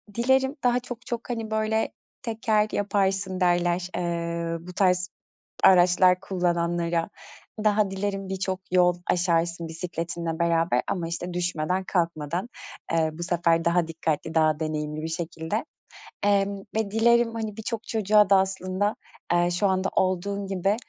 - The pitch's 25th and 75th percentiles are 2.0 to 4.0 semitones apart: Yes, average, 3.3 semitones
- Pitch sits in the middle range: Yes, medium, 180 Hz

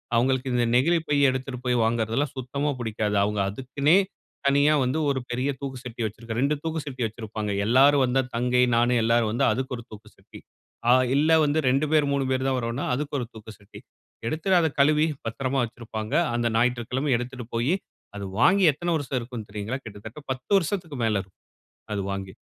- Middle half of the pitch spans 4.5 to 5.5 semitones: No, average, 3.8 semitones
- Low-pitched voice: Yes, low, 125 Hz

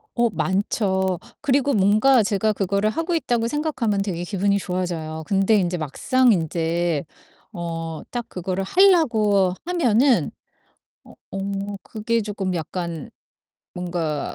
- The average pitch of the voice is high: Yes, high, 200 Hz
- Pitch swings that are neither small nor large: Yes, average, 4.7 semitones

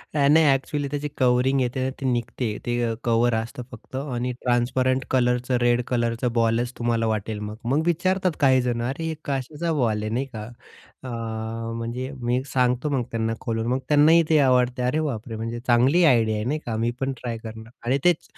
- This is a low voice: Yes, low, 125 Hz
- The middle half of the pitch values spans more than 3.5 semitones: No, narrow, 2.6 semitones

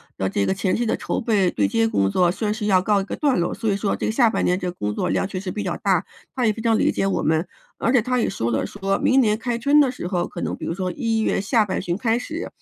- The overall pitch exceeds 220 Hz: No, high, 200 Hz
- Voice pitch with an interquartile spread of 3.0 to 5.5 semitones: Yes, average, 4.3 semitones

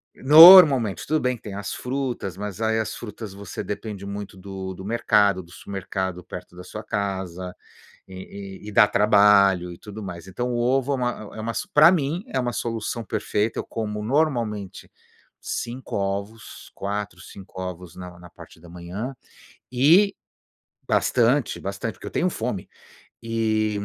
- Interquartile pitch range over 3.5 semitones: Yes, average, 3.9 semitones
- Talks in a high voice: No, low, 105 Hz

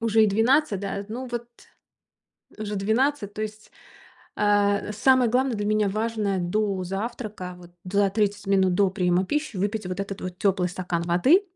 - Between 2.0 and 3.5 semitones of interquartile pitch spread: Yes, narrow, 2.6 semitones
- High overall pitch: Yes, high, 205 Hz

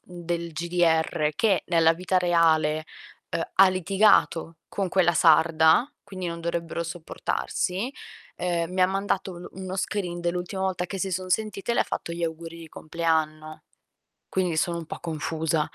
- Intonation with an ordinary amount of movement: No, narrow, 2.3 semitones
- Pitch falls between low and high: Yes, medium, 170 Hz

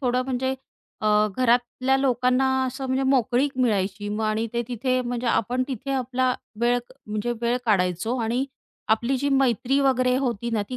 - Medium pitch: No, high, 245 Hz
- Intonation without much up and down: Yes, narrow, 2.3 semitones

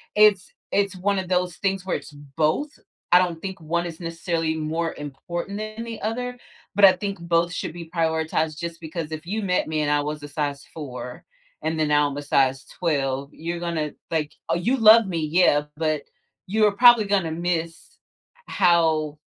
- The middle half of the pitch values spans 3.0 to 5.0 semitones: Yes, average, 3.7 semitones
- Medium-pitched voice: Yes, medium, 170 Hz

